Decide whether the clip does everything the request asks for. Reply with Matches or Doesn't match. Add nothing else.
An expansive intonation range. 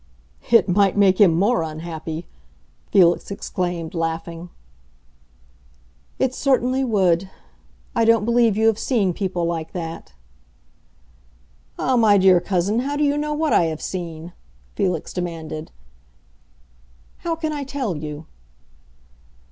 Matches